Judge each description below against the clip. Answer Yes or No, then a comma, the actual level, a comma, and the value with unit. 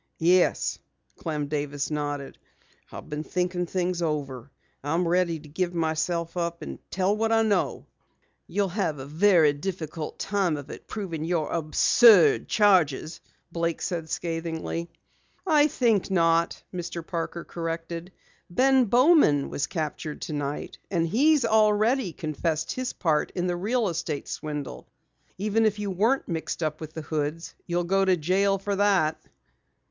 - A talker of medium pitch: Yes, medium, 170 Hz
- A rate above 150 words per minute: No, average, 145 wpm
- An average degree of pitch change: Yes, average, 4.0 semitones